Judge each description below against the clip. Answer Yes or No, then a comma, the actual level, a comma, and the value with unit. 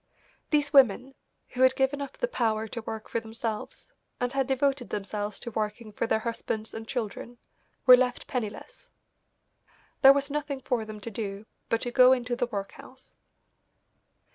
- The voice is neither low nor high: No, high, 240 Hz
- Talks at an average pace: Yes, average, 165 wpm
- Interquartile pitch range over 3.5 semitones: No, average, 3.2 semitones